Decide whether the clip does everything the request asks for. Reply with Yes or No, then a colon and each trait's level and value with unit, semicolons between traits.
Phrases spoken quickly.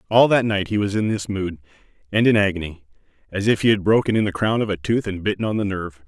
Yes: fast, 265 wpm